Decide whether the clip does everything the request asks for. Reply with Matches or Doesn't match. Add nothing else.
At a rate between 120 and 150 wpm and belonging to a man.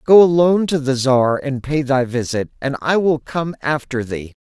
Doesn't match